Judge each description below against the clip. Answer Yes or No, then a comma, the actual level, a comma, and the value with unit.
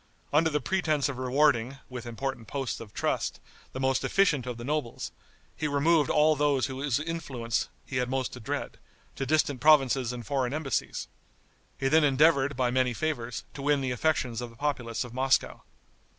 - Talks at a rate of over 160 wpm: Yes, average, 180 wpm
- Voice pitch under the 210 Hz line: Yes, low, 135 Hz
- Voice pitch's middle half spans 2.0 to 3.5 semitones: Yes, average, 3.2 semitones